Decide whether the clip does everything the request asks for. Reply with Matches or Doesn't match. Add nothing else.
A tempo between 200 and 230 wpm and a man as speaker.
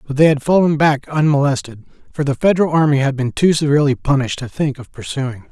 Matches